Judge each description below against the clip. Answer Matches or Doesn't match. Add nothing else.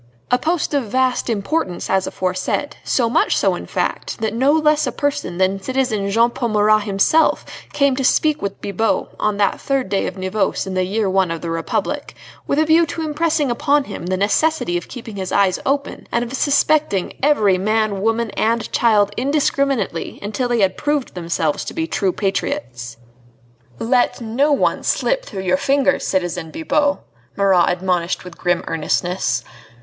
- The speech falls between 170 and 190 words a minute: Matches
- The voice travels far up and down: Matches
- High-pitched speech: Matches